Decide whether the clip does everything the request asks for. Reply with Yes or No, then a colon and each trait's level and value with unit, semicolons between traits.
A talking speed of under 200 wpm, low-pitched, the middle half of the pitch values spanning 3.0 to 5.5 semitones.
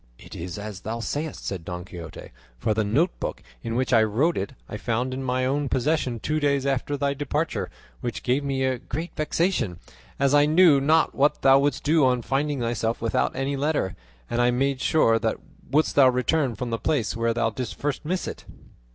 No: fast, 205 wpm; low, 130 Hz; average, 3.9 semitones